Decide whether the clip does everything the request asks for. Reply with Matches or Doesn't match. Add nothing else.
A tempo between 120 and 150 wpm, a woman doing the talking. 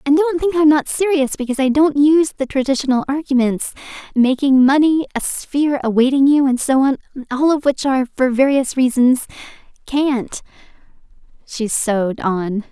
Matches